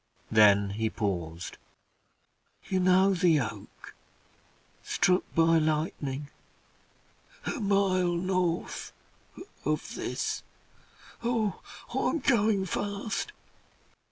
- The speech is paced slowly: Yes, slow, 80 wpm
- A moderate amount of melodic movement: No, wide, 6.9 semitones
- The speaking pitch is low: No, medium, 180 Hz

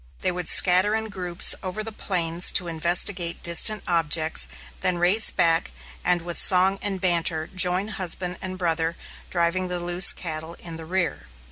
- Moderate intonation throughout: No, narrow, 1.7 semitones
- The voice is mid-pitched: Yes, medium, 180 Hz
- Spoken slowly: No, average, 160 wpm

